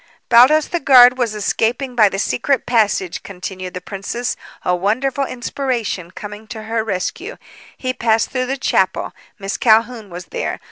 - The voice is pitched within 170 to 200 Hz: No, high, 225 Hz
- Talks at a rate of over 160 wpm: No, average, 155 wpm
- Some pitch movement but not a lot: Yes, average, 4.1 semitones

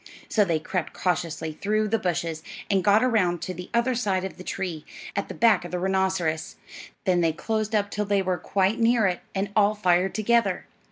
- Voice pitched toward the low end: No, high, 190 Hz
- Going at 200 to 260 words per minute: Yes, fast, 205 wpm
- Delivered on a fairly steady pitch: No, average, 3.1 semitones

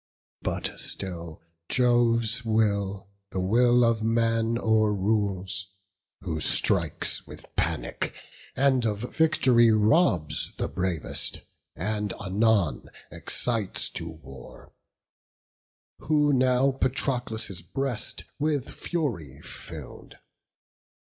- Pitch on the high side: No, low, 110 Hz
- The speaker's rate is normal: No, slow, 90 wpm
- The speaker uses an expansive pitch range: No, average, 4.3 semitones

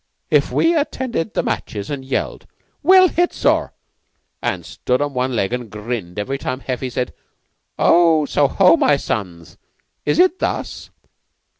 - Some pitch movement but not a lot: No, wide, 7.0 semitones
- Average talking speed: Yes, average, 145 wpm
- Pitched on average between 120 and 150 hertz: Yes, low, 135 Hz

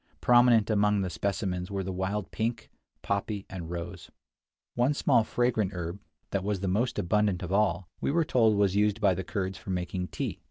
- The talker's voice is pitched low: Yes, low, 100 Hz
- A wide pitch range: No, average, 2.8 semitones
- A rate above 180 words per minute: Yes, average, 190 wpm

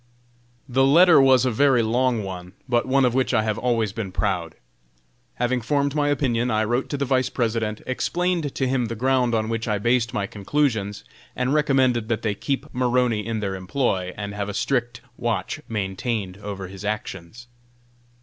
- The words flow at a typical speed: Yes, average, 180 wpm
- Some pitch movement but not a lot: Yes, average, 3.7 semitones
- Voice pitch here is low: Yes, low, 120 Hz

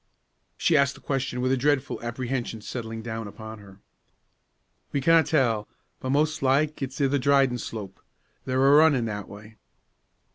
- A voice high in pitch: No, low, 130 Hz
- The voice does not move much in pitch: No, average, 3.8 semitones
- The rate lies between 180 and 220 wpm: No, average, 160 wpm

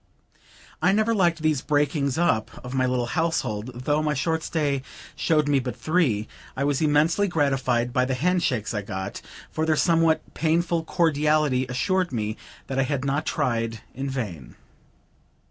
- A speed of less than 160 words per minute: No, average, 165 wpm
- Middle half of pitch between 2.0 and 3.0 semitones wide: No, average, 4.3 semitones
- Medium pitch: Yes, medium, 145 Hz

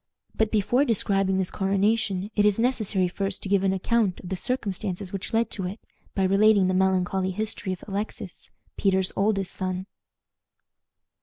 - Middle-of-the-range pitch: No, high, 195 Hz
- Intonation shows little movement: Yes, narrow, 2.1 semitones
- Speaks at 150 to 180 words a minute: Yes, average, 160 wpm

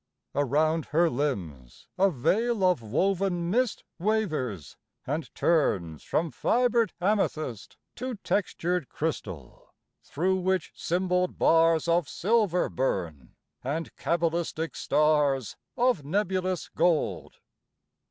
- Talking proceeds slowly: Yes, slow, 100 wpm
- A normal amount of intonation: Yes, average, 4.9 semitones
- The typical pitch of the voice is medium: Yes, medium, 165 Hz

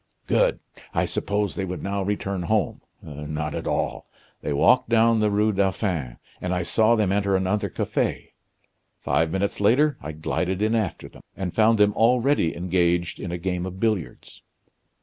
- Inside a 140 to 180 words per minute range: Yes, average, 170 wpm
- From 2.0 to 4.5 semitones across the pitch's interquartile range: Yes, average, 3.5 semitones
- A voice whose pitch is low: Yes, very low, 95 Hz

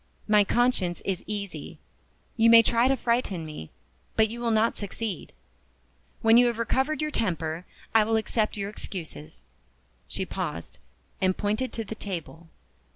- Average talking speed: Yes, average, 155 wpm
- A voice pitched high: Yes, high, 215 Hz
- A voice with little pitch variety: No, average, 4.0 semitones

